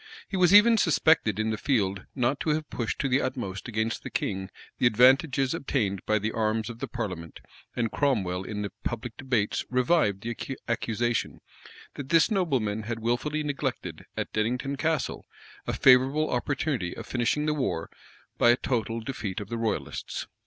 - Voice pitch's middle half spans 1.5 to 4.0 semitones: No, average, 4.5 semitones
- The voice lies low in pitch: Yes, low, 120 Hz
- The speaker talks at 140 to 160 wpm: No, average, 170 wpm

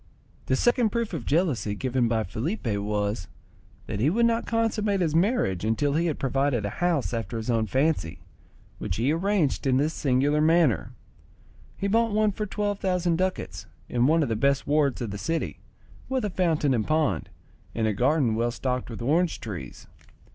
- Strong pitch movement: Yes, wide, 7.6 semitones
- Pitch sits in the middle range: Yes, medium, 145 Hz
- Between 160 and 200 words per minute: Yes, average, 185 wpm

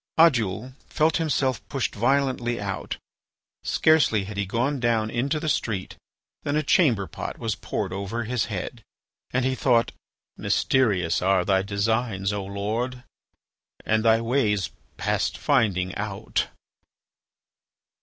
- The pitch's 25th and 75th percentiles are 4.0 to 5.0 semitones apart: Yes, average, 4.4 semitones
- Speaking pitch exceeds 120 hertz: No, low, 115 Hz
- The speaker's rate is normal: No, slow, 125 wpm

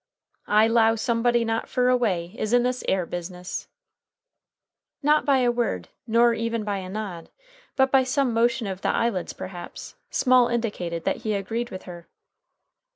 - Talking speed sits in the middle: Yes, average, 160 wpm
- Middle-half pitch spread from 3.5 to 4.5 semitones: Yes, average, 4.2 semitones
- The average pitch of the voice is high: Yes, high, 225 Hz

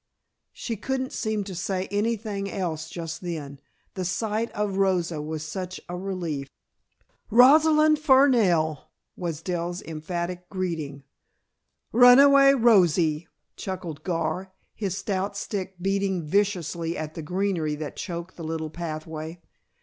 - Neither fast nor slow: No, slow, 120 wpm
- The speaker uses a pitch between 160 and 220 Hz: Yes, medium, 185 Hz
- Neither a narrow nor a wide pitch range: Yes, average, 4.0 semitones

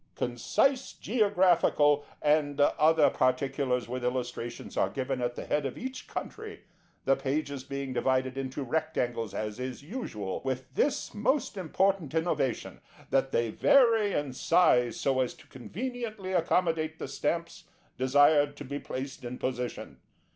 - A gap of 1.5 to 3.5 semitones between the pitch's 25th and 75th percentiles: No, average, 5.2 semitones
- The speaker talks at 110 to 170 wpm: Yes, average, 140 wpm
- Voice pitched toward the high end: No, medium, 140 Hz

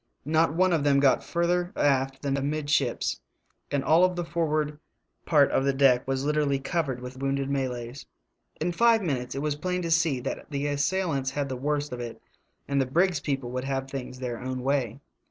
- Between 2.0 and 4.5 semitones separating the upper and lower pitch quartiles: Yes, average, 3.0 semitones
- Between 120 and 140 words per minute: No, average, 195 wpm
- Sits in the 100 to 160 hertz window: Yes, medium, 140 Hz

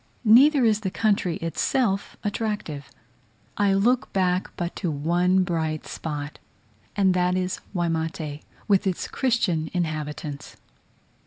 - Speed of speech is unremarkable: No, slow, 115 wpm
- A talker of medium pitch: Yes, medium, 180 Hz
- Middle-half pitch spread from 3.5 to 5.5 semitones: Yes, average, 4.4 semitones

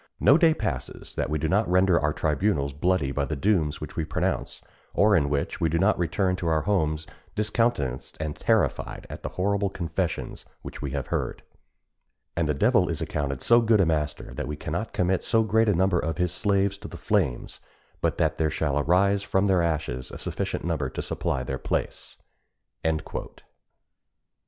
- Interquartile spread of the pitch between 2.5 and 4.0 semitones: No, average, 4.8 semitones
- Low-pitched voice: Yes, very low, 85 Hz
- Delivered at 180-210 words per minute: Yes, average, 185 wpm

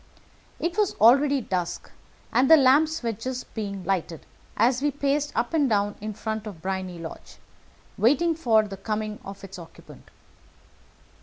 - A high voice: Yes, high, 220 Hz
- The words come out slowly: No, average, 155 wpm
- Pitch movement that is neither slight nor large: No, wide, 6.0 semitones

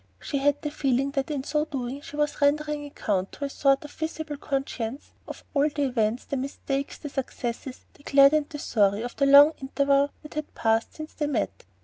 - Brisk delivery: Yes, fast, 210 wpm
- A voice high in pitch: Yes, very high, 280 Hz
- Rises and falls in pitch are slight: Yes, narrow, 2.0 semitones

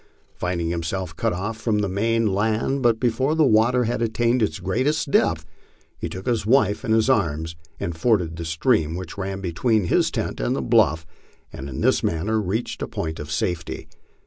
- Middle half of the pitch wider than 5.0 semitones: Yes, wide, 5.5 semitones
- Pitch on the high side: No, low, 100 Hz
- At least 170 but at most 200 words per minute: Yes, average, 190 wpm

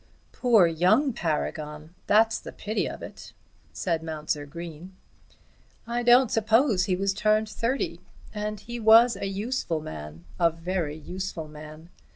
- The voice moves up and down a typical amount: No, wide, 5.7 semitones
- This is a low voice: No, high, 190 Hz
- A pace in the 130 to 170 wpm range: Yes, average, 140 wpm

